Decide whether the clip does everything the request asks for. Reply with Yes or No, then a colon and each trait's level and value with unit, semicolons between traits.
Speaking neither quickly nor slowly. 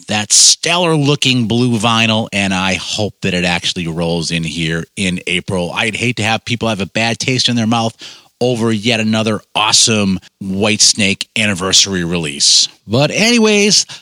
Yes: average, 165 wpm